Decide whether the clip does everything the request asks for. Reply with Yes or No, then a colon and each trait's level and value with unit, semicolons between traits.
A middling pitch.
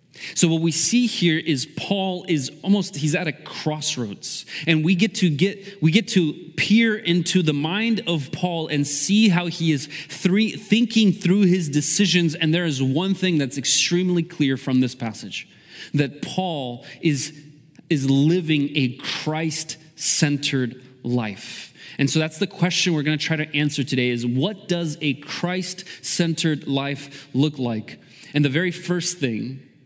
Yes: medium, 160 Hz